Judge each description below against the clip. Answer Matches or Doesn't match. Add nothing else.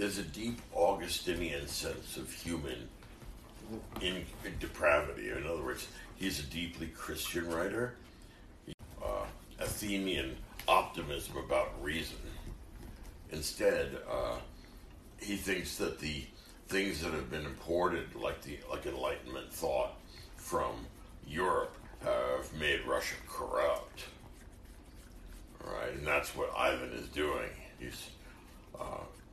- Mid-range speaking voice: Doesn't match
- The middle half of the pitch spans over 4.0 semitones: Matches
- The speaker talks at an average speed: Doesn't match